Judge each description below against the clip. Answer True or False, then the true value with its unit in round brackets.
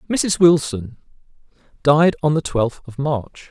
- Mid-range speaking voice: True (145 Hz)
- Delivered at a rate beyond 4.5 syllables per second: False (3.8 syllables/s)